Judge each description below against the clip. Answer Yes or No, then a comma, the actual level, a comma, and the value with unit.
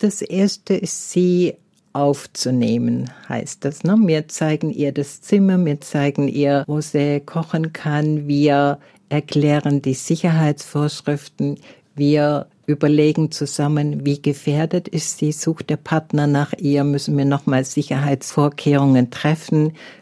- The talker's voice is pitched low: No, medium, 150 Hz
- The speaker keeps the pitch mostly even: Yes, narrow, 1.9 semitones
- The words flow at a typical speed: No, slow, 120 wpm